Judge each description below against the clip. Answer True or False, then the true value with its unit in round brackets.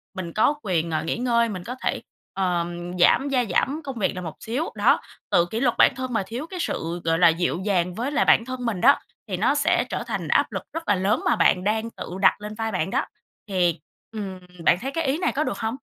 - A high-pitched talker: True (210 Hz)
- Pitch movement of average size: False (6.0 semitones)